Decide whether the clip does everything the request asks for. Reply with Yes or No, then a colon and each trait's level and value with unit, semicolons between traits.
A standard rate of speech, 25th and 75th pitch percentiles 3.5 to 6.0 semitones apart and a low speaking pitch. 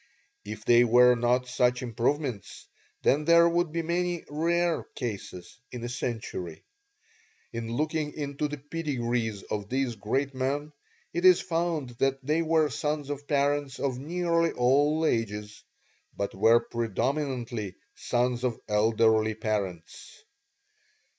No: slow, 125 wpm; average, 4.9 semitones; low, 130 Hz